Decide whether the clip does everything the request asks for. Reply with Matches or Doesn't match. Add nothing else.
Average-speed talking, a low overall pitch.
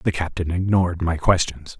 Matches